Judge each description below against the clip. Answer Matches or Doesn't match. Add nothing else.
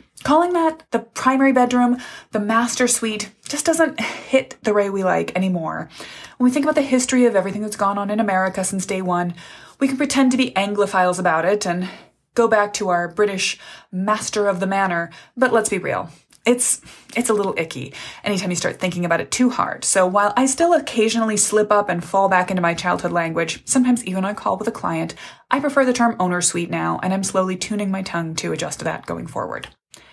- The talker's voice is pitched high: Matches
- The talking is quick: Matches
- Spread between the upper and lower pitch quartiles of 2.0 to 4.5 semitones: Doesn't match